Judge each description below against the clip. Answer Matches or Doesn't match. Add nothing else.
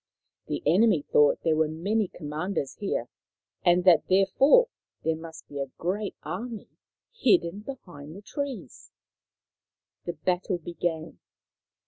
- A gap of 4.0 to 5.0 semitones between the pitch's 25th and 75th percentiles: Matches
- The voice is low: Doesn't match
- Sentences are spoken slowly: Matches